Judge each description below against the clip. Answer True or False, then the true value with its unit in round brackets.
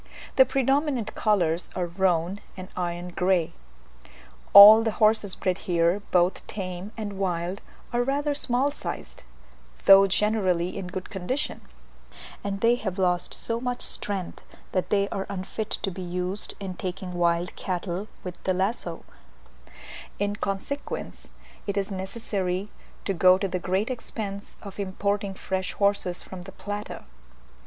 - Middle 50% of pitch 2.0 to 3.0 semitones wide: True (2.5 semitones)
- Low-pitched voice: False (195 Hz)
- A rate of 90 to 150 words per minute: True (140 wpm)